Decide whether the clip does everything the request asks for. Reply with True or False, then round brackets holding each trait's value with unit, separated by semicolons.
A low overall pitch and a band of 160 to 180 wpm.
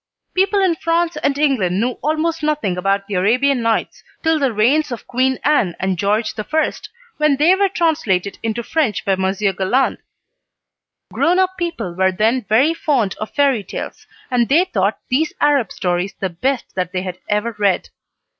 False (240 Hz; 175 wpm)